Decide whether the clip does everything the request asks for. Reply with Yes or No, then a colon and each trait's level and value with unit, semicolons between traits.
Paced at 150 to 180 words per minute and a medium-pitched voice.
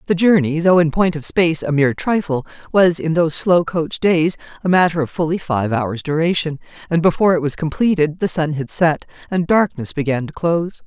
No: average, 200 wpm; medium, 165 Hz